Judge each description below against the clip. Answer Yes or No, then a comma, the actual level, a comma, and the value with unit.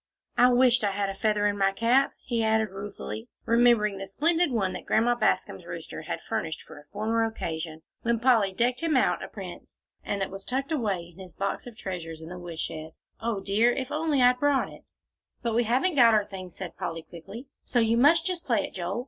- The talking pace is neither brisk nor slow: No, fast, 215 wpm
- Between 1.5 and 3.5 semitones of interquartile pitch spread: No, average, 4.1 semitones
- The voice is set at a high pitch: Yes, high, 220 Hz